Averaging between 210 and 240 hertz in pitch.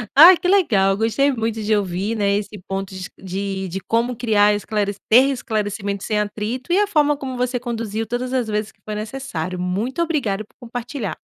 Yes: high, 220 Hz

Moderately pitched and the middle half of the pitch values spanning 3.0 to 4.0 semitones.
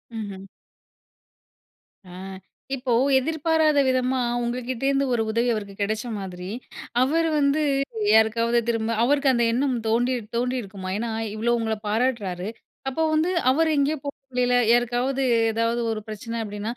No: high, 240 Hz; average, 3.4 semitones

